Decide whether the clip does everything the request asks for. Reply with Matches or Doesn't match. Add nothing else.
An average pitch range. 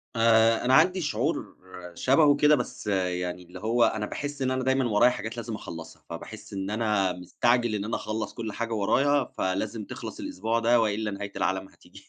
Matches